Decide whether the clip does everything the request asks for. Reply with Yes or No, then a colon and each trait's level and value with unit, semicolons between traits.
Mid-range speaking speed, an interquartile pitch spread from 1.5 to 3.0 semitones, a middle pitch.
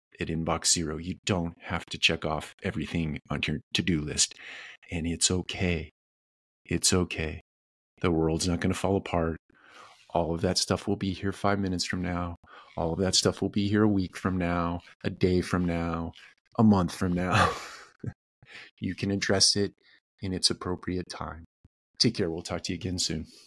No: average, 185 wpm; narrow, 2.5 semitones; very low, 90 Hz